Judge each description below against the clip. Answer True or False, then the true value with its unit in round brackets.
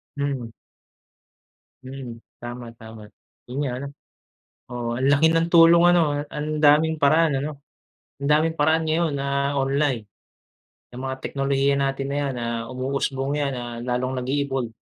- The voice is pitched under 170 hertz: True (140 Hz)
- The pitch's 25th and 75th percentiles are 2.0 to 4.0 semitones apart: True (2.7 semitones)